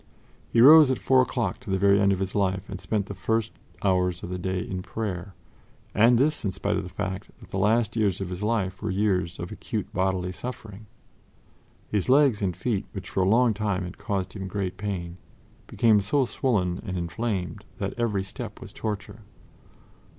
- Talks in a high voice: No, low, 100 Hz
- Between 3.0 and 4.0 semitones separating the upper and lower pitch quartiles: Yes, average, 3.3 semitones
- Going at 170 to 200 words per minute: Yes, average, 195 wpm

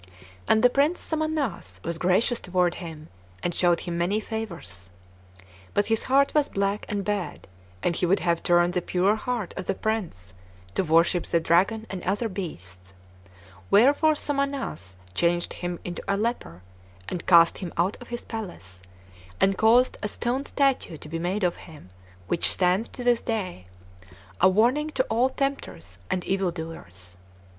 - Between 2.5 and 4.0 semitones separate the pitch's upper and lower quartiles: No, average, 5.1 semitones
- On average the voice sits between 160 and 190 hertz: Yes, medium, 185 Hz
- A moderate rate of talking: Yes, average, 165 wpm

